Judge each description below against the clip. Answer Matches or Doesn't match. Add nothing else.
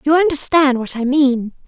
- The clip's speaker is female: Matches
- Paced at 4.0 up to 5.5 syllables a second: Matches